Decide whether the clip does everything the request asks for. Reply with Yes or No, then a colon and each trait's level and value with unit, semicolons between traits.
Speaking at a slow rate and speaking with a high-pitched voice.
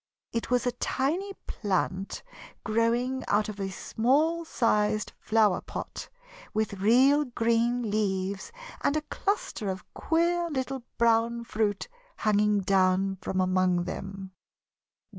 Yes: slow, 120 wpm; high, 225 Hz